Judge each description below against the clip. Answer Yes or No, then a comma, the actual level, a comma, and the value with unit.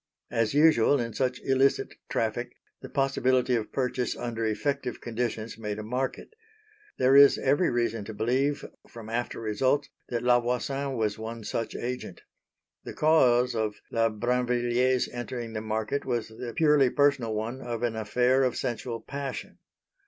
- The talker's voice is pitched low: Yes, low, 120 Hz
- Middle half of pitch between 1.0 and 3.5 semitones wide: Yes, narrow, 2.6 semitones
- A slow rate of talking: No, average, 150 wpm